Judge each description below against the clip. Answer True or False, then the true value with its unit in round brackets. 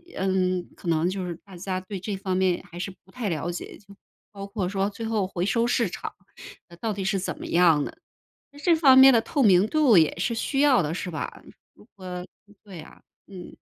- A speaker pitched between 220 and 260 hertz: False (195 Hz)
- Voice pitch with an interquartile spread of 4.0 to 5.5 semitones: False (3.5 semitones)